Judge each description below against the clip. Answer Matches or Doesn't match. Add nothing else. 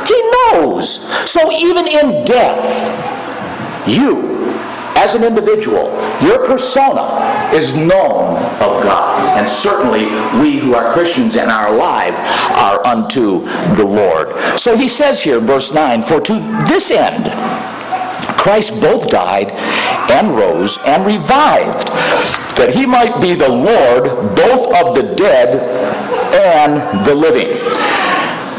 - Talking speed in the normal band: Doesn't match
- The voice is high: Matches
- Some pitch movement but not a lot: Doesn't match